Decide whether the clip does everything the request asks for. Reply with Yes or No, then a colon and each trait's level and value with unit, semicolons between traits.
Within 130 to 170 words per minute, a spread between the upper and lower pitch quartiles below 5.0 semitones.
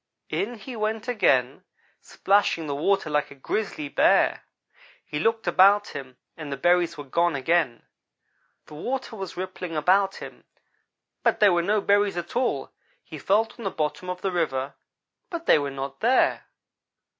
No: average, 165 wpm; wide, 5.6 semitones